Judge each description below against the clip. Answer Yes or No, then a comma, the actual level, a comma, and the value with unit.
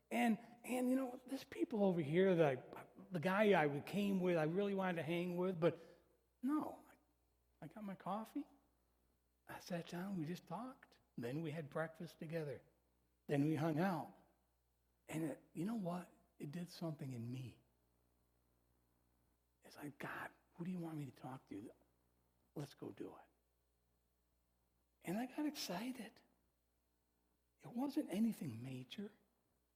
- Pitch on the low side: No, medium, 160 Hz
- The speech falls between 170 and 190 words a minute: No, average, 155 wpm